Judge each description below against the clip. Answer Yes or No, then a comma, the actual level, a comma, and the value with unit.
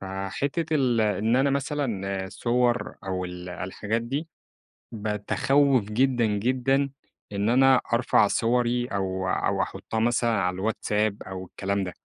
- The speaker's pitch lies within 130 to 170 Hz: No, low, 110 Hz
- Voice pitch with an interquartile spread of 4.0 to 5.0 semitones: Yes, average, 4.5 semitones